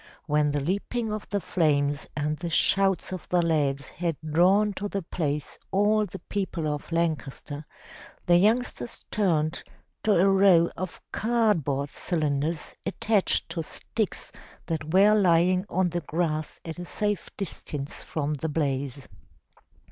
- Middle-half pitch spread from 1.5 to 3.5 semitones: No, average, 4.5 semitones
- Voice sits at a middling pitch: Yes, medium, 170 Hz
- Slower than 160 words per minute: Yes, average, 140 wpm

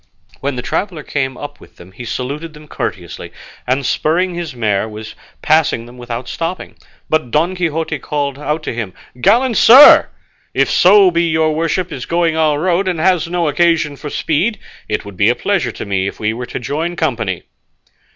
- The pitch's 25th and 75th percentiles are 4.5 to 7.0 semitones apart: Yes, wide, 5.6 semitones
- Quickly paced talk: No, average, 190 wpm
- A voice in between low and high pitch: Yes, medium, 150 Hz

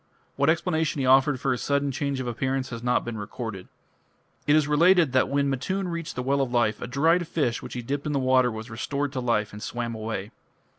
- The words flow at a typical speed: No, fast, 230 wpm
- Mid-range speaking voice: No, low, 130 Hz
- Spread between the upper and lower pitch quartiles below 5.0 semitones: Yes, average, 3.4 semitones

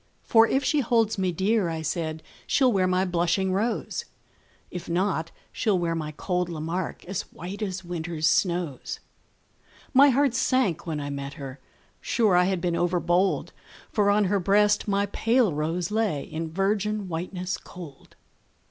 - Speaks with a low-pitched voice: No, medium, 185 Hz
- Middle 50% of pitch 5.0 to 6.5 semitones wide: No, average, 3.7 semitones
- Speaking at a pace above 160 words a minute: No, average, 155 wpm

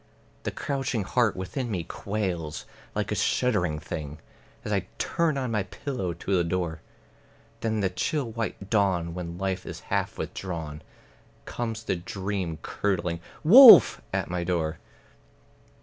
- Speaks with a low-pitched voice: Yes, very low, 95 Hz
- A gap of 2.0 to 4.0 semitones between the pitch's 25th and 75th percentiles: No, average, 4.7 semitones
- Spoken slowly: No, average, 145 wpm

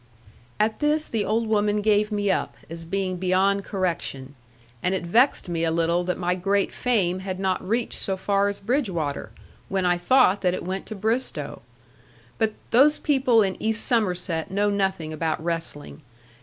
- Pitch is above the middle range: Yes, high, 195 Hz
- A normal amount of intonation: Yes, average, 3.4 semitones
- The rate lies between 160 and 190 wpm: Yes, average, 170 wpm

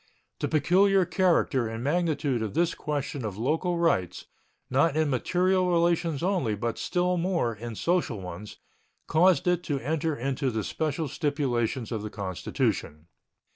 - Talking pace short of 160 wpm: Yes, average, 145 wpm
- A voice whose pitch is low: No, medium, 145 Hz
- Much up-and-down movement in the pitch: Yes, wide, 6.8 semitones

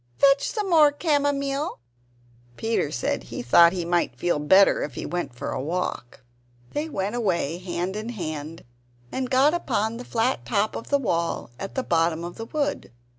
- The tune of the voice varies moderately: No, wide, 8.4 semitones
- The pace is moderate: Yes, average, 175 wpm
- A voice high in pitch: Yes, high, 200 Hz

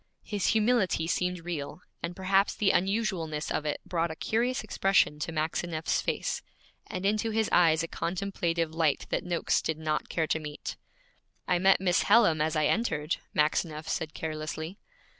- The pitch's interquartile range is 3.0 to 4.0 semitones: Yes, average, 3.6 semitones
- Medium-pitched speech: Yes, medium, 170 Hz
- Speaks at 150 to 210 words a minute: Yes, average, 160 wpm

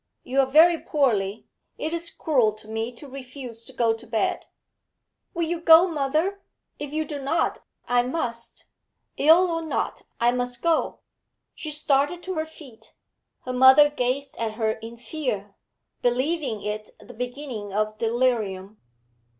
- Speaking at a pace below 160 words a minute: Yes, average, 150 wpm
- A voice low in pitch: No, very high, 255 Hz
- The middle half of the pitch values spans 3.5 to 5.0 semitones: No, wide, 5.4 semitones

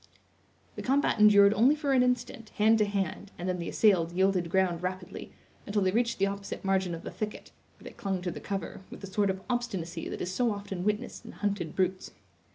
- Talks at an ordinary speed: No, fast, 215 wpm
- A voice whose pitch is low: No, high, 200 Hz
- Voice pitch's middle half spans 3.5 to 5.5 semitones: No, narrow, 2.5 semitones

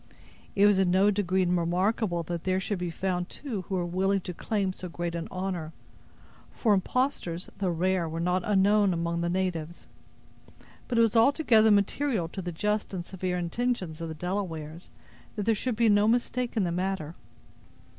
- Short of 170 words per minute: No, average, 180 wpm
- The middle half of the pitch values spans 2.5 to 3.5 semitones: Yes, average, 3.2 semitones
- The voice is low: No, medium, 185 Hz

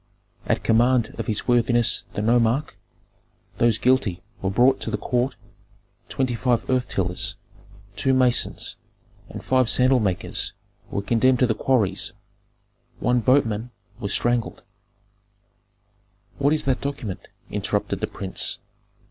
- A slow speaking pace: Yes, slow, 130 wpm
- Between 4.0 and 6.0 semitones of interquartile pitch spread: No, average, 3.5 semitones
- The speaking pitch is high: No, low, 120 Hz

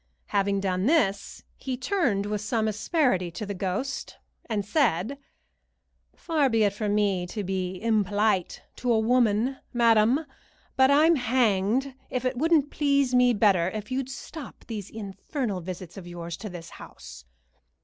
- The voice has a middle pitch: No, high, 215 Hz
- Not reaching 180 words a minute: Yes, average, 150 wpm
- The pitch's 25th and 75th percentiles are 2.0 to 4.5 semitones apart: No, average, 4.9 semitones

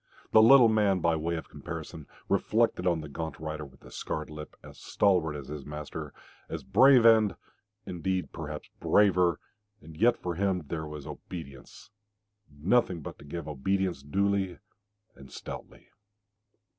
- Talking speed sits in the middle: Yes, average, 150 wpm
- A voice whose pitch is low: Yes, very low, 85 Hz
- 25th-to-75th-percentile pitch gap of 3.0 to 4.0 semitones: No, average, 4.4 semitones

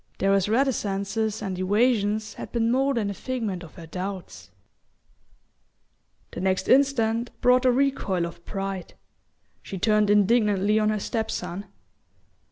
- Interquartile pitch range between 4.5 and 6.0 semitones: No, average, 3.3 semitones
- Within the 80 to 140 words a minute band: Yes, slow, 135 wpm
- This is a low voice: No, high, 210 Hz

